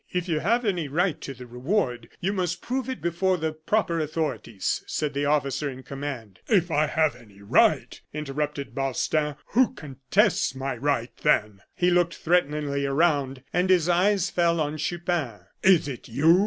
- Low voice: No, medium, 155 Hz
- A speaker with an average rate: Yes, average, 170 wpm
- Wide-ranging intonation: No, average, 4.4 semitones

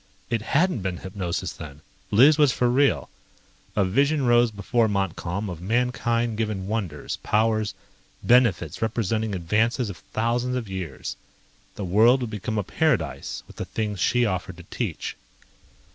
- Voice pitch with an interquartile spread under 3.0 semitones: No, average, 4.3 semitones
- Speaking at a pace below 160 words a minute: Yes, average, 145 wpm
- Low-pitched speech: Yes, low, 110 Hz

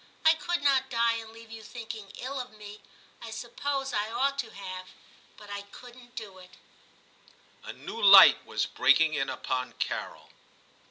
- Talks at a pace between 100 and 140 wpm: No, average, 165 wpm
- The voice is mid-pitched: No, high, 230 Hz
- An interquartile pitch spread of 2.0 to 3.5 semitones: No, average, 4.1 semitones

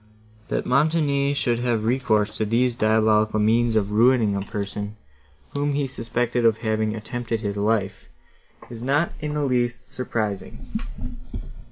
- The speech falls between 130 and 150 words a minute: Yes, average, 140 wpm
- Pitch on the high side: No, low, 115 Hz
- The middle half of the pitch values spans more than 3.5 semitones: No, average, 2.9 semitones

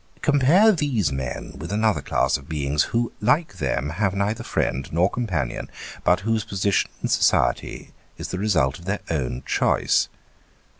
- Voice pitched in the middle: No, low, 100 Hz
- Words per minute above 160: No, average, 155 wpm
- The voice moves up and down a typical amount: No, wide, 7.6 semitones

